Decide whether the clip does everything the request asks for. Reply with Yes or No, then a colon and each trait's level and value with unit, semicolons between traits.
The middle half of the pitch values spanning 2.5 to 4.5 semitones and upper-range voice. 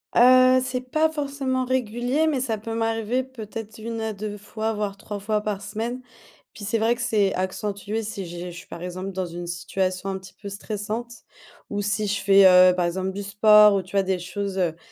Yes: average, 3.2 semitones; high, 210 Hz